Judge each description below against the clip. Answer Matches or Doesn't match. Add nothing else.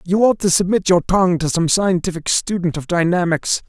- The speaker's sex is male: Matches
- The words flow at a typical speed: Matches